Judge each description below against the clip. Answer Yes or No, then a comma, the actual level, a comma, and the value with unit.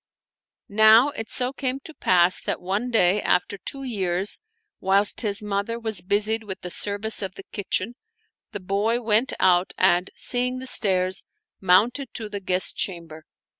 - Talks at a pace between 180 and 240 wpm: No, average, 160 wpm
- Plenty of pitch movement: No, average, 3.6 semitones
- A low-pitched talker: No, high, 205 Hz